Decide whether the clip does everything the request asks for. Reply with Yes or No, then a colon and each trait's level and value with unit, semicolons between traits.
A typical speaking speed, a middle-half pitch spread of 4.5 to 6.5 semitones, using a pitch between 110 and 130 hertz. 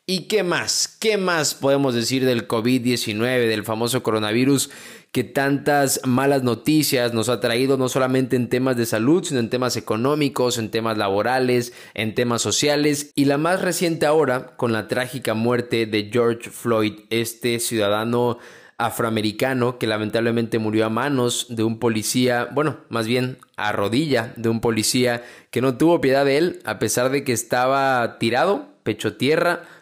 No: average, 160 wpm; average, 3.0 semitones; low, 125 Hz